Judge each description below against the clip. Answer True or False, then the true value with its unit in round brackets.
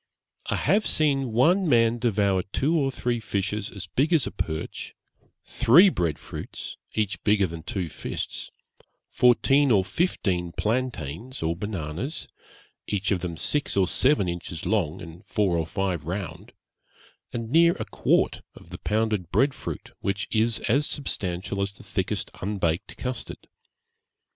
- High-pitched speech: False (105 Hz)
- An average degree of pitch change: False (5.8 semitones)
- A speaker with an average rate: True (150 wpm)